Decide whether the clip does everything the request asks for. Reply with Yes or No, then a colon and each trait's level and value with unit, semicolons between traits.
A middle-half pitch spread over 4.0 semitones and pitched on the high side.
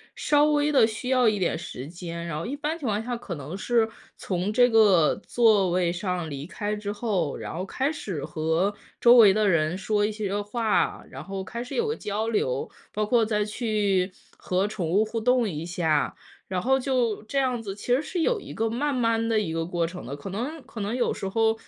Yes: average, 4.8 semitones; high, 210 Hz